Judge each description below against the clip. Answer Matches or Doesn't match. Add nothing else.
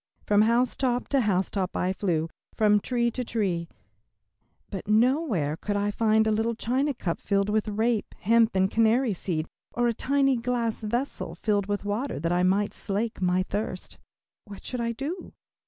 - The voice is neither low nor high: Doesn't match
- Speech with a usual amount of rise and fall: Matches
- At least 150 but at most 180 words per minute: Matches